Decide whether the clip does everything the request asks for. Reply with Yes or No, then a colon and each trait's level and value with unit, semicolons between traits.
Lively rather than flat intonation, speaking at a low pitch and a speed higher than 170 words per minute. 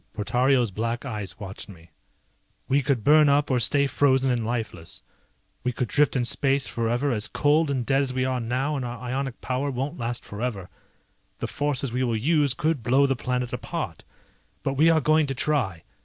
No: average, 3.2 semitones; low, 130 Hz; average, 190 wpm